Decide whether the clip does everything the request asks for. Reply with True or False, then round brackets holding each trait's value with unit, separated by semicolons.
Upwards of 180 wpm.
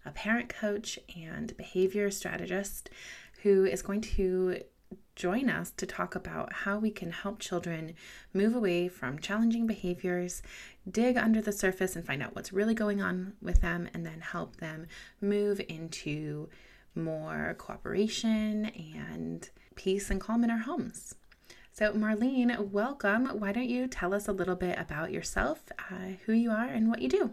False (160 wpm)